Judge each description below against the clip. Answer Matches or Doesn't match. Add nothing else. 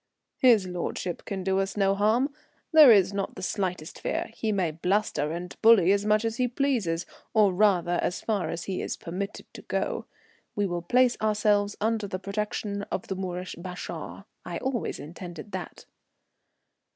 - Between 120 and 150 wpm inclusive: Doesn't match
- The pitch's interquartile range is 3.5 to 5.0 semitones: Doesn't match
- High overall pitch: Matches